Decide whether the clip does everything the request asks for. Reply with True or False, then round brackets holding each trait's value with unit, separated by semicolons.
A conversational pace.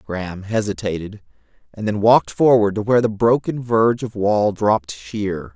True (160 wpm)